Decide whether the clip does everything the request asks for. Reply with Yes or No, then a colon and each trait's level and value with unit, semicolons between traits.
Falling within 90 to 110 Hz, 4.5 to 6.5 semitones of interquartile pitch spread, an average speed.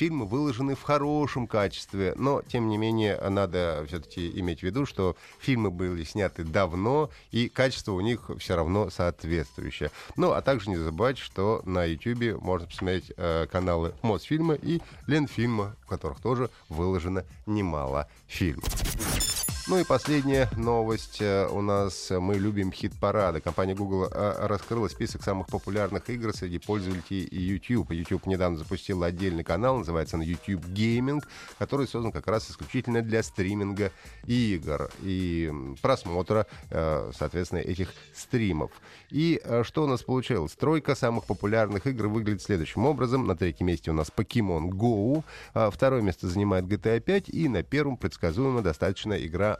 Yes: low, 100 Hz; average, 4.8 semitones; average, 145 wpm